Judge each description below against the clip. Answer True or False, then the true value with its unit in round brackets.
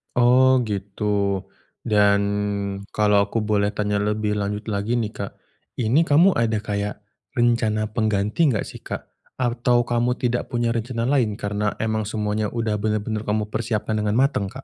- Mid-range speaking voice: False (110 Hz)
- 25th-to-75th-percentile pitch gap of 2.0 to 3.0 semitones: True (2.4 semitones)